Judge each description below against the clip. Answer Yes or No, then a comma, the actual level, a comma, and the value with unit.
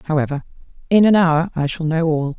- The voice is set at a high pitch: No, medium, 160 Hz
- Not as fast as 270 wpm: Yes, average, 200 wpm